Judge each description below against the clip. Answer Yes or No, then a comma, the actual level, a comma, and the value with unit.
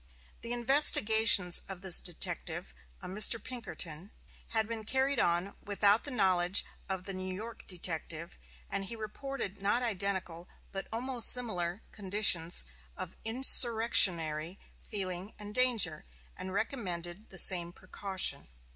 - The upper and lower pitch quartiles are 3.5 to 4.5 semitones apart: Yes, average, 4.1 semitones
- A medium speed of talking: No, slow, 125 wpm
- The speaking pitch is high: Yes, high, 200 Hz